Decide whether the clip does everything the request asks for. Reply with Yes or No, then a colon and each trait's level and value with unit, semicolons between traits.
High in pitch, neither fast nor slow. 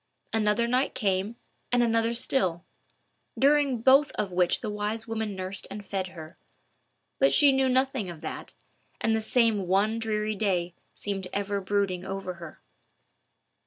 Yes: high, 210 Hz; average, 150 wpm